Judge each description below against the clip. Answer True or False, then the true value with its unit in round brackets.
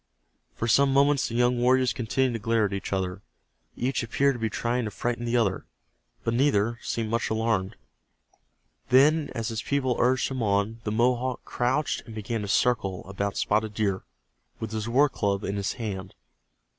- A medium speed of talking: True (180 wpm)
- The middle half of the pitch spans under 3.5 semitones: True (3.1 semitones)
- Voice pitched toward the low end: True (115 Hz)